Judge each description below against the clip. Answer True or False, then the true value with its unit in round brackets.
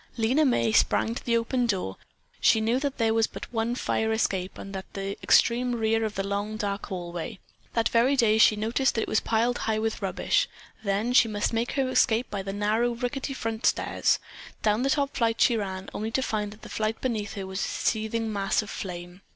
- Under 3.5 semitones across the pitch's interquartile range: True (2.6 semitones)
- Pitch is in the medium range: False (220 Hz)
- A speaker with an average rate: False (220 wpm)